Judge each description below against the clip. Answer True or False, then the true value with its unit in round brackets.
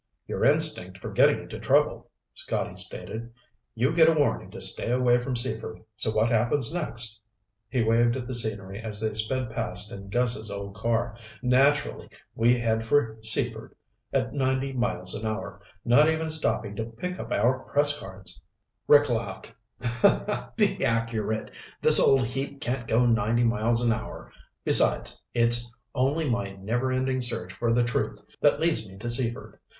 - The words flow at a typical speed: True (165 wpm)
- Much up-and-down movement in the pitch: False (2.9 semitones)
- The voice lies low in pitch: True (120 Hz)